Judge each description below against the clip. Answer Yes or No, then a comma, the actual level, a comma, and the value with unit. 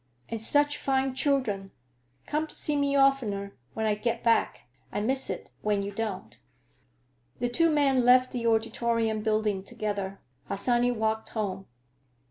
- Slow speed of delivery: No, average, 145 wpm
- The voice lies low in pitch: No, high, 230 Hz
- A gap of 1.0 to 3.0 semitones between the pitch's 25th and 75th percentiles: No, average, 4.1 semitones